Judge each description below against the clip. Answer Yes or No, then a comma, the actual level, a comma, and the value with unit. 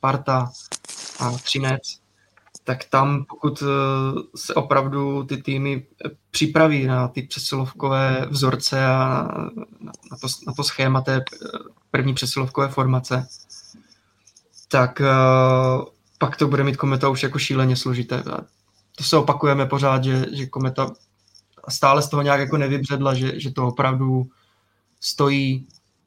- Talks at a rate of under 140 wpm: Yes, average, 120 wpm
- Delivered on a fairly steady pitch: Yes, narrow, 1.3 semitones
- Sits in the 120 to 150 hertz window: Yes, low, 135 Hz